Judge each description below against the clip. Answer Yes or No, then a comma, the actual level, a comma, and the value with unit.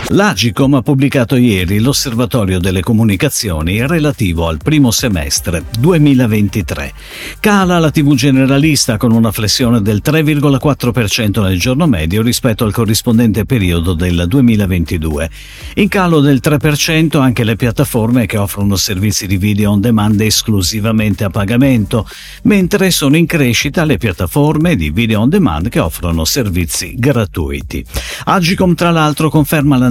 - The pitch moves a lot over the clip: Yes, wide, 6.2 semitones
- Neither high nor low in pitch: No, low, 115 Hz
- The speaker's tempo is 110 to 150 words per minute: Yes, average, 130 wpm